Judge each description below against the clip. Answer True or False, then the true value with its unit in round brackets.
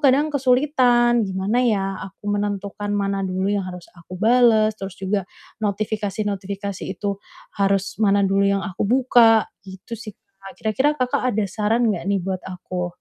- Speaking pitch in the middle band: False (205 Hz)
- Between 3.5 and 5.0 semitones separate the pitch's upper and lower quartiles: False (2.7 semitones)